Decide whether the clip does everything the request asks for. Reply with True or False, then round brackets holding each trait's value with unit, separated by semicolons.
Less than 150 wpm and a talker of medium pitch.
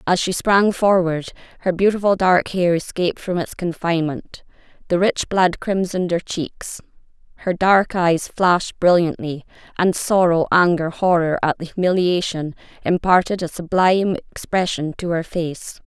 True (140 wpm; 175 Hz)